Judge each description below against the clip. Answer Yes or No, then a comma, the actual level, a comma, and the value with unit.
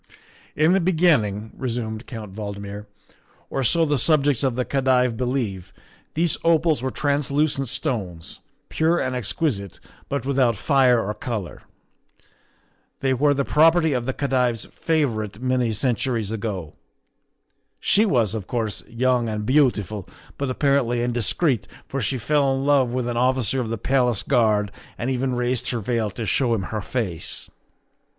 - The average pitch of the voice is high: No, low, 125 Hz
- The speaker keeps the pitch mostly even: No, average, 4.0 semitones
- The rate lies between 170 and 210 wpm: No, average, 155 wpm